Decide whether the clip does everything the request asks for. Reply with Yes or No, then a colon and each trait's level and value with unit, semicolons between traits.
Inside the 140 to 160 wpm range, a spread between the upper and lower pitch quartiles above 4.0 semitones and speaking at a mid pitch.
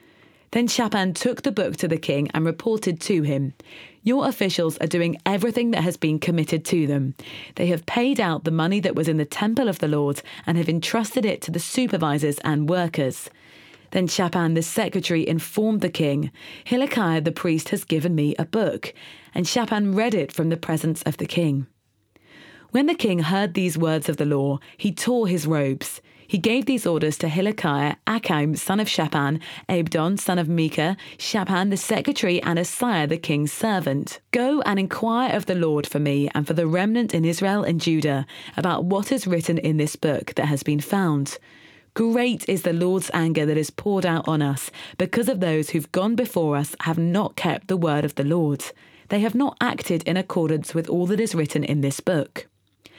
No: average, 195 wpm; average, 4.7 semitones; medium, 170 Hz